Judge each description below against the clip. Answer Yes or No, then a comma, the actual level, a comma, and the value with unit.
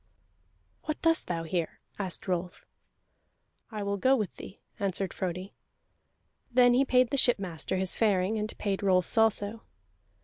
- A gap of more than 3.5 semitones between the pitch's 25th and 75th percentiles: Yes, average, 3.9 semitones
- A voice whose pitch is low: No, high, 200 Hz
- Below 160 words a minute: Yes, average, 140 wpm